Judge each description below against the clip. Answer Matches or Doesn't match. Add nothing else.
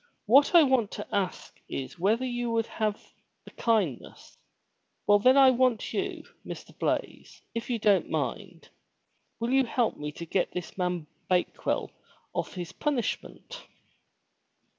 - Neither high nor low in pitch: Doesn't match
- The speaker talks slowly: Doesn't match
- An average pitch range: Doesn't match